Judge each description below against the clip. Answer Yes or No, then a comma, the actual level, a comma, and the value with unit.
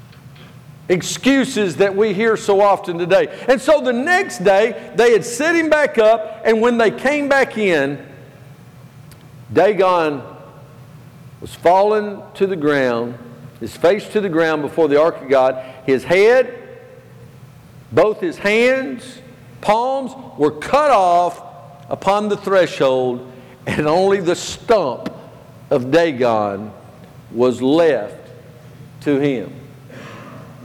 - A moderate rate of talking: No, slow, 120 wpm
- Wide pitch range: Yes, wide, 8.0 semitones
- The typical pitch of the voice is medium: Yes, medium, 160 Hz